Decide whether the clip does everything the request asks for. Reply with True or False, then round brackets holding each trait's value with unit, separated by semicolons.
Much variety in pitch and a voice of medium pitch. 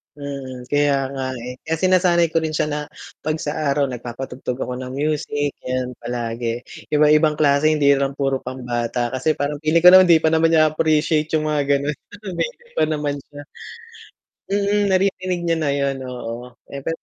False (3.2 semitones; 145 Hz)